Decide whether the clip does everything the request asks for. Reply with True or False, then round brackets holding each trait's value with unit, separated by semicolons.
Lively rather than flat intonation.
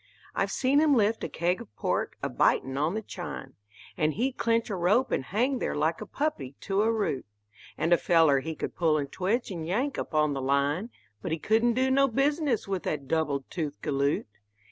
True (7.7 semitones)